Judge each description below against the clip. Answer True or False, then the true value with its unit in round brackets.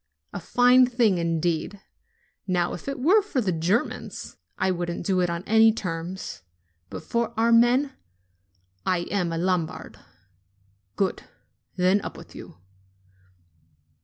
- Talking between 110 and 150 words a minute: True (135 wpm)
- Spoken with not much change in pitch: False (5.4 semitones)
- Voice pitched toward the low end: False (185 Hz)